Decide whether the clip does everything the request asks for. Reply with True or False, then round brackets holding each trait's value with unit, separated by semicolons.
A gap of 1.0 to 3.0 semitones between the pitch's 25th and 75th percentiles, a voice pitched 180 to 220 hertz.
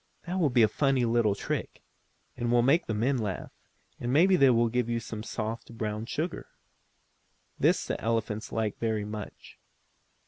False (2.7 semitones; 115 Hz)